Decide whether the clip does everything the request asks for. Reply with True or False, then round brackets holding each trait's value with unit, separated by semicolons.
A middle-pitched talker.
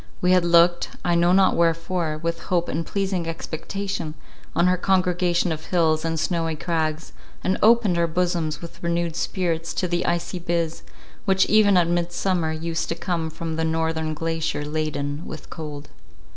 True (170 Hz)